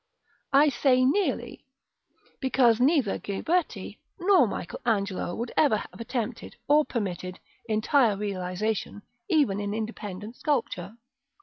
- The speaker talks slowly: Yes, slow, 110 wpm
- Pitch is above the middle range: Yes, high, 225 Hz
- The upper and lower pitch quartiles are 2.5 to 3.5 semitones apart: No, average, 5.3 semitones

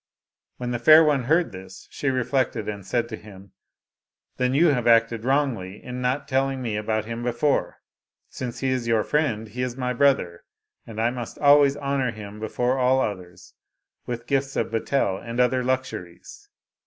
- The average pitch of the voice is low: Yes, low, 125 Hz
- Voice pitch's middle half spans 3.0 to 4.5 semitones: Yes, average, 3.5 semitones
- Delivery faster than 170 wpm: Yes, average, 180 wpm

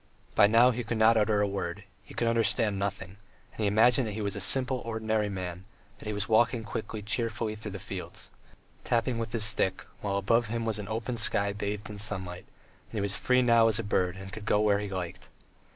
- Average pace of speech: No, fast, 225 wpm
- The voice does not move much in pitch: Yes, narrow, 2.3 semitones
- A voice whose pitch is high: No, low, 105 Hz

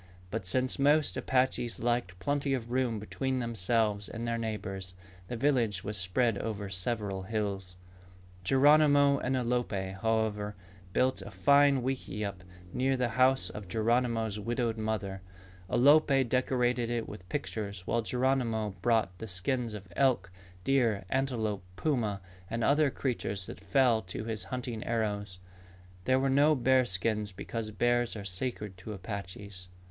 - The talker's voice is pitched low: Yes, low, 115 Hz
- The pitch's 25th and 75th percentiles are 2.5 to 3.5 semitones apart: No, average, 4.2 semitones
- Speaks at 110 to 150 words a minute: Yes, average, 140 wpm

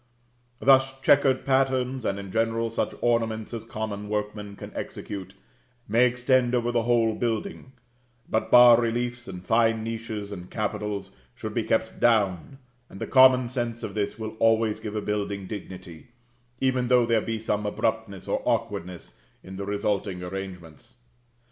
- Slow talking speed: No, average, 155 wpm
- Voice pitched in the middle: No, low, 110 Hz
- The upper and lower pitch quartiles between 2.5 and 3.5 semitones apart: Yes, average, 3.0 semitones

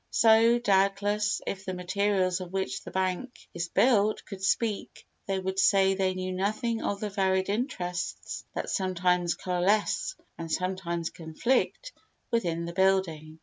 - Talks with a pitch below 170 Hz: No, high, 190 Hz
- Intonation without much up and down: Yes, narrow, 2.3 semitones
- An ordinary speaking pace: Yes, average, 145 wpm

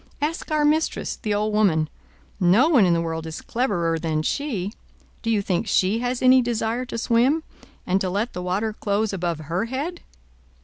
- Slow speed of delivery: No, average, 185 wpm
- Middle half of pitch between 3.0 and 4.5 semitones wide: No, wide, 5.6 semitones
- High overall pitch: Yes, high, 215 Hz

